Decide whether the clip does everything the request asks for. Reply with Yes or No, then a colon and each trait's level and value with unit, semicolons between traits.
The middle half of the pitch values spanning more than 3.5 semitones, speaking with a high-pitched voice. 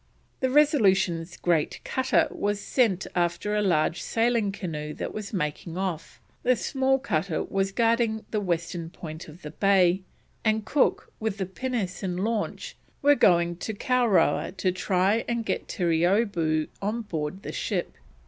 Yes: average, 4.5 semitones; high, 195 Hz